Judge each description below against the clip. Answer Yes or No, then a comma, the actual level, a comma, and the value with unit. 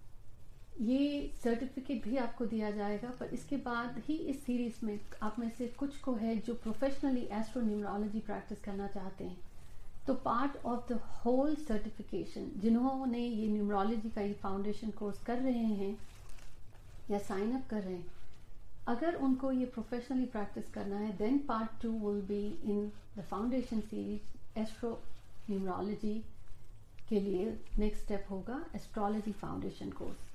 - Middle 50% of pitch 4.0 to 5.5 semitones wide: No, average, 3.5 semitones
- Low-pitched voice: No, high, 215 Hz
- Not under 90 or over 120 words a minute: No, average, 145 wpm